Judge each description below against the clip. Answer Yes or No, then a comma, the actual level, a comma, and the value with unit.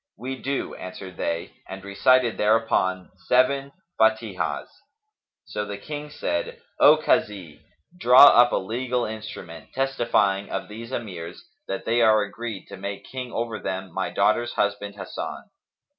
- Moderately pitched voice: No, low, 110 Hz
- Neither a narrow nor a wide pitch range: Yes, average, 3.9 semitones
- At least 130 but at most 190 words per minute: Yes, average, 140 wpm